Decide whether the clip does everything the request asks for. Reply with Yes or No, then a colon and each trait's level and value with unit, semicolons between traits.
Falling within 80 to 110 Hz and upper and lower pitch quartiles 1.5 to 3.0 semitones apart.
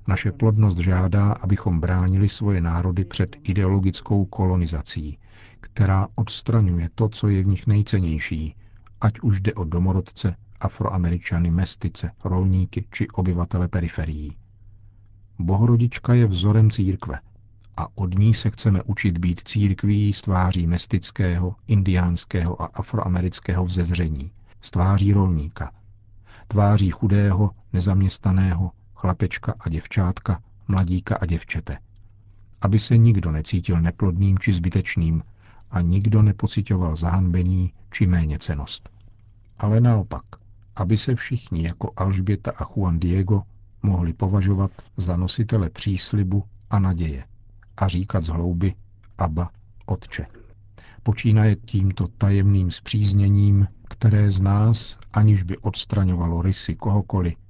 Yes: low, 100 Hz; narrow, 2.4 semitones